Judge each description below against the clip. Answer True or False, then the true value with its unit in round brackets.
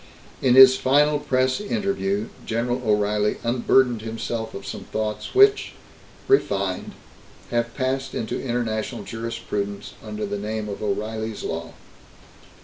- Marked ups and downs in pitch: False (3.5 semitones)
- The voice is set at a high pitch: False (115 Hz)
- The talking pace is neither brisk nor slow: False (120 wpm)